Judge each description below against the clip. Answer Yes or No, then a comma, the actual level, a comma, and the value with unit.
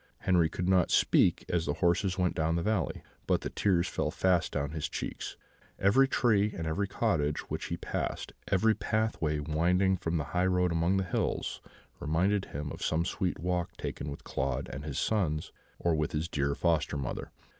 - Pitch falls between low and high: No, very low, 85 Hz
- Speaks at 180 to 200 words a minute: Yes, average, 185 wpm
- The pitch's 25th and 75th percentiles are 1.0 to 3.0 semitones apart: No, average, 3.5 semitones